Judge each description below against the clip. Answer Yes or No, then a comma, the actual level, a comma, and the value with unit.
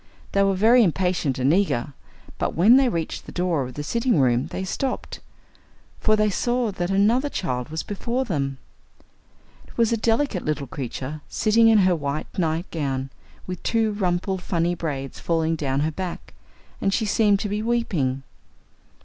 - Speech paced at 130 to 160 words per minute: No, average, 170 wpm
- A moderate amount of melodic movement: No, wide, 6.5 semitones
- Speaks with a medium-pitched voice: Yes, medium, 180 Hz